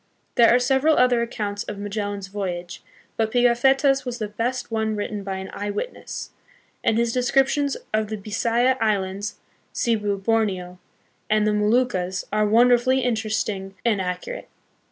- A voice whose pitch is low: No, high, 220 Hz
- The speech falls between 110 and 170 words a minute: Yes, average, 155 wpm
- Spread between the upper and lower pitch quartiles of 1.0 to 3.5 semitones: Yes, average, 3.2 semitones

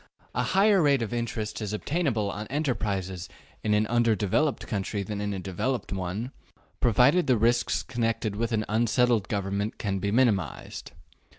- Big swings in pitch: No, average, 3.3 semitones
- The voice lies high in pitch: No, low, 110 Hz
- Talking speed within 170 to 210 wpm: No, average, 155 wpm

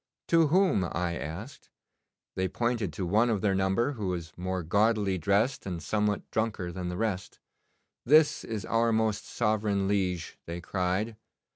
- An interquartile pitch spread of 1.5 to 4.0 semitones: Yes, average, 3.7 semitones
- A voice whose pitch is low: Yes, low, 100 Hz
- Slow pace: No, average, 155 wpm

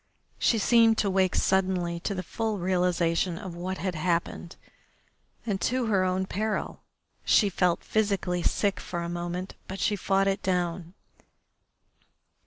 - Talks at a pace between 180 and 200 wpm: No, average, 145 wpm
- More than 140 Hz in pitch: Yes, medium, 185 Hz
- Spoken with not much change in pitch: Yes, narrow, 2.3 semitones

